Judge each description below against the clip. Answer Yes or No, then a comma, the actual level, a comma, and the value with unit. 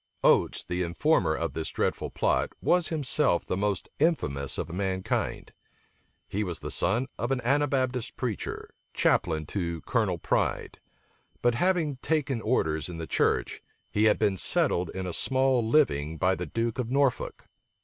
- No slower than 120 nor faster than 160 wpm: Yes, average, 155 wpm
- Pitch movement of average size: No, wide, 7.3 semitones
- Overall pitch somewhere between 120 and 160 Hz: No, low, 110 Hz